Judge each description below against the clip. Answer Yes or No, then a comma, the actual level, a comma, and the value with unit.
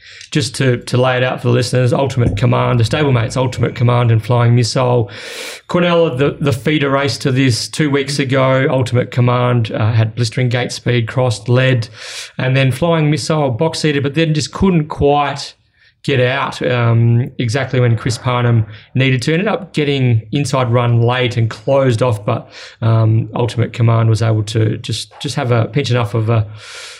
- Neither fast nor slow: Yes, average, 180 wpm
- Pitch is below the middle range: Yes, low, 125 Hz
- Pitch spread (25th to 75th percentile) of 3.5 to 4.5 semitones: No, average, 3.0 semitones